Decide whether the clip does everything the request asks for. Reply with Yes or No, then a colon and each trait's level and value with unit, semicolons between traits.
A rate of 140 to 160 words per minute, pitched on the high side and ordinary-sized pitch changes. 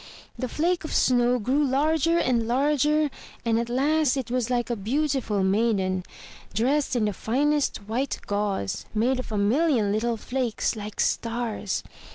Yes: average, 155 wpm; high, 245 Hz; average, 4.5 semitones